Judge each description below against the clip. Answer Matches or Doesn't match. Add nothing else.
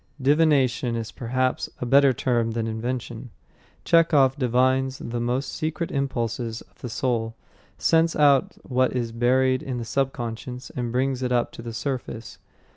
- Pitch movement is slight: Matches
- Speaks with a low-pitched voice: Matches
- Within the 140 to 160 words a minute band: Matches